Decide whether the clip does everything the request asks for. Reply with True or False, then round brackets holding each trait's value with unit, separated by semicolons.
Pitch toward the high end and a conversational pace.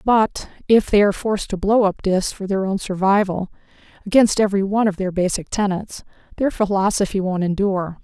True (195 Hz; 165 wpm)